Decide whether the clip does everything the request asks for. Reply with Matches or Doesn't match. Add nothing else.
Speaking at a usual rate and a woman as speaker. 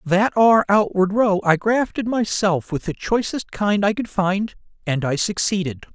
Doesn't match